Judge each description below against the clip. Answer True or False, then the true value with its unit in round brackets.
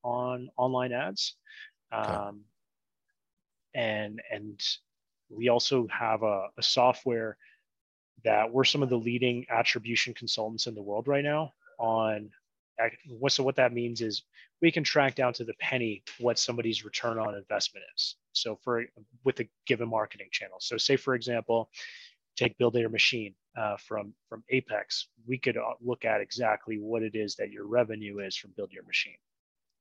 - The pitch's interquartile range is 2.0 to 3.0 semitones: True (2.5 semitones)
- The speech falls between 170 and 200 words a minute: False (160 wpm)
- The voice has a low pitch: True (120 Hz)